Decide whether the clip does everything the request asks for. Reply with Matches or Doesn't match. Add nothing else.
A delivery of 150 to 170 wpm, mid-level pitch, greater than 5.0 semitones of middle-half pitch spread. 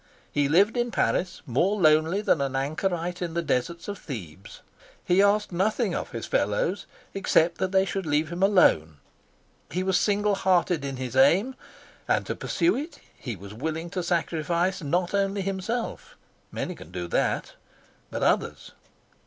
Matches